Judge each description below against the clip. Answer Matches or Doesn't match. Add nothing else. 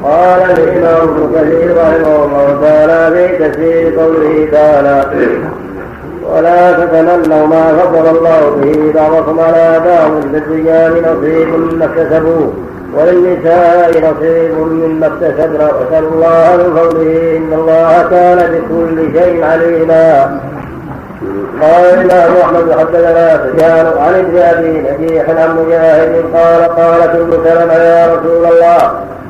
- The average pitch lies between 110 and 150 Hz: Doesn't match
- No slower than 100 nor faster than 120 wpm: Matches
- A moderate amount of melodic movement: Doesn't match